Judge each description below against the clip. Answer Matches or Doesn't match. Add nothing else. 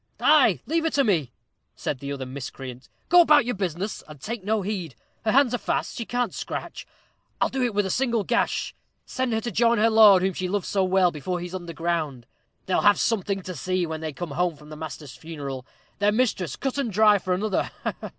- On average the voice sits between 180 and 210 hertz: Matches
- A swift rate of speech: Matches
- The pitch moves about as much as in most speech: Doesn't match